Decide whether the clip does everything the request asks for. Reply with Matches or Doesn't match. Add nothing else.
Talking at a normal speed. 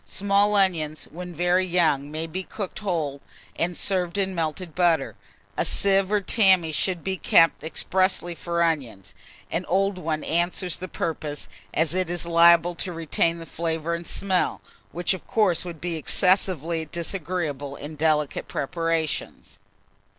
Matches